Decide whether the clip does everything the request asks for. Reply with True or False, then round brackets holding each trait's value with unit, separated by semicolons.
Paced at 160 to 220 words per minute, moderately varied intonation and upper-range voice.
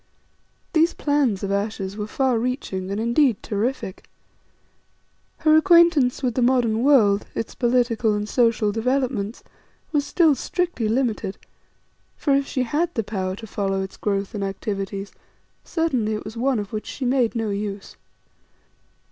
False (150 wpm; 4.6 semitones; 230 Hz)